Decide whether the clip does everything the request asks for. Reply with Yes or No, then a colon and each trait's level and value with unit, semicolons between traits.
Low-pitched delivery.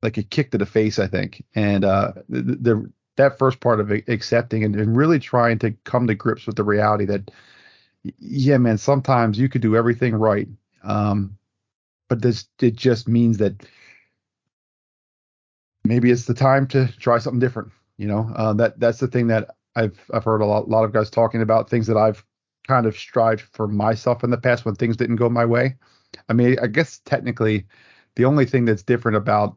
Yes: low, 115 Hz